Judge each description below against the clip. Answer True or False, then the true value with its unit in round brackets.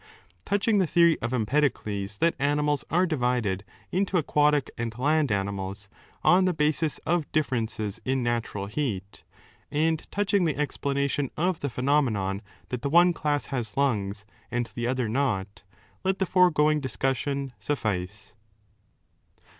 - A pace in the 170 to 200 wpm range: False (140 wpm)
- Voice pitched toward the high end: False (140 Hz)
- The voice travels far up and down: True (5.8 semitones)